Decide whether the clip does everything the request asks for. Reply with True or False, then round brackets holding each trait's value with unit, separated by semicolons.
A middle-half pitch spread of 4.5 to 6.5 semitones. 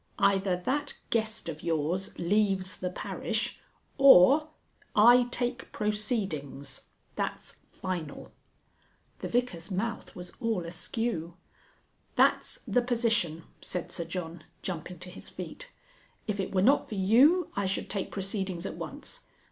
True (4.8 semitones)